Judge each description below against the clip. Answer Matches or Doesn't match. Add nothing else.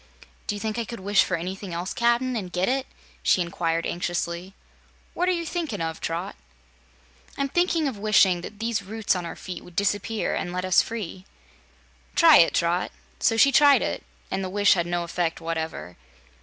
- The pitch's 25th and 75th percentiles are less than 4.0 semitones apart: Doesn't match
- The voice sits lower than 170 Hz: Doesn't match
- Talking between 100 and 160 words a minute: Doesn't match